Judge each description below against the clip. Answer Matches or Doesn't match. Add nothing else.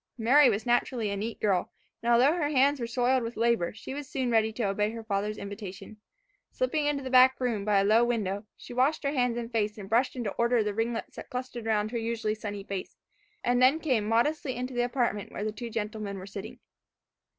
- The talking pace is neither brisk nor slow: Doesn't match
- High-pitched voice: Matches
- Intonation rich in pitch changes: Doesn't match